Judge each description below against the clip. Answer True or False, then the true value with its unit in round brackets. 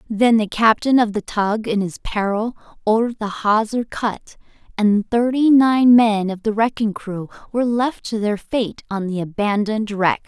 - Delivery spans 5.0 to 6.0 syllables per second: False (4.6 syllables/s)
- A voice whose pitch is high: True (220 Hz)